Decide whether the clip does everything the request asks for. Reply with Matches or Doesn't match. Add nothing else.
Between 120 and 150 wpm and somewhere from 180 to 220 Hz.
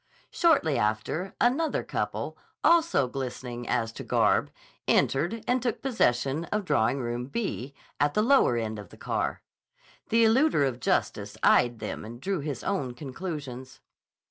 Doesn't match